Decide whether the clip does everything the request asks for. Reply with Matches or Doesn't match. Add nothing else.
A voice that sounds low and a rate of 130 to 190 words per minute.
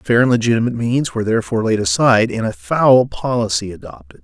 Matches